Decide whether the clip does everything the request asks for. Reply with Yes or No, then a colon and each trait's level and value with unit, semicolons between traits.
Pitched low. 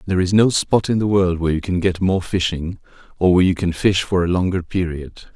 Yes: very low, 90 Hz